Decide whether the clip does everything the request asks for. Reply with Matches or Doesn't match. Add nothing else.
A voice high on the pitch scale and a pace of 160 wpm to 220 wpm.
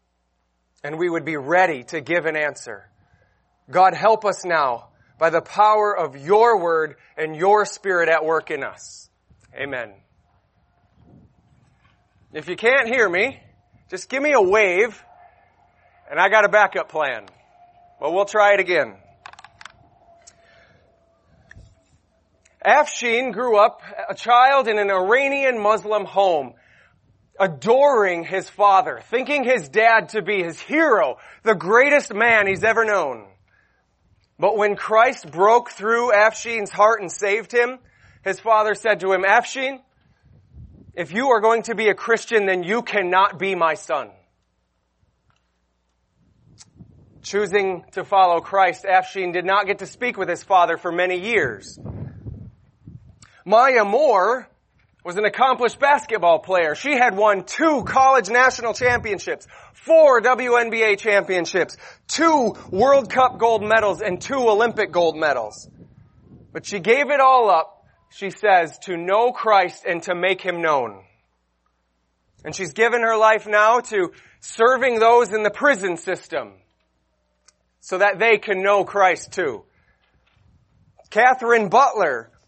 Doesn't match